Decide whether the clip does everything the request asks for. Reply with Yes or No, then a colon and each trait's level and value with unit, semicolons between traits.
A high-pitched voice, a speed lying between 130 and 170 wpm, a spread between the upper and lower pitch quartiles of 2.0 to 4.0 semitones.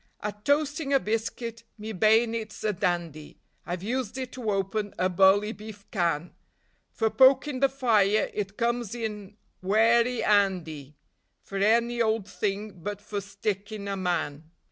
Yes: high, 210 Hz; average, 145 wpm; average, 2.9 semitones